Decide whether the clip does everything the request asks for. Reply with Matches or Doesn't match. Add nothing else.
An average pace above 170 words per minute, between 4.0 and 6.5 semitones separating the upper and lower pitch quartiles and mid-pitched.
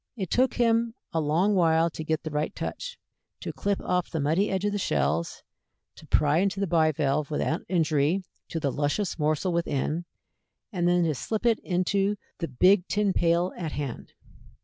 Matches